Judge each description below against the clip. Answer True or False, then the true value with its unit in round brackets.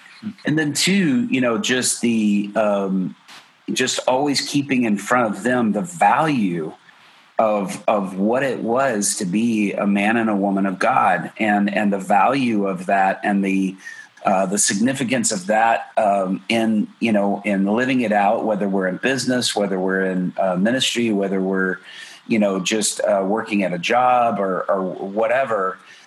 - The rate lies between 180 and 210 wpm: False (170 wpm)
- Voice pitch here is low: True (105 Hz)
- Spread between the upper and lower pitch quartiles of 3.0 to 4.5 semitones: True (3.7 semitones)